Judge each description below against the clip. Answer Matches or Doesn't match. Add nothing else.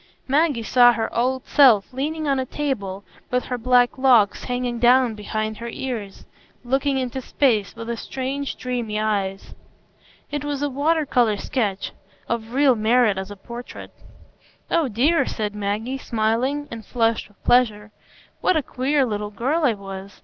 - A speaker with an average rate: Matches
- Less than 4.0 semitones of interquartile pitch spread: Matches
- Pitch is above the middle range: Matches